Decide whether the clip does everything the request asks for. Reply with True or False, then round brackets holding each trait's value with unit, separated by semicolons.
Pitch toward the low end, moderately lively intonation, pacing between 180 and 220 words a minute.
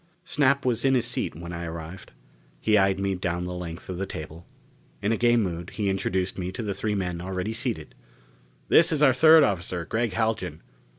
True (95 Hz; 4.8 semitones; 200 wpm)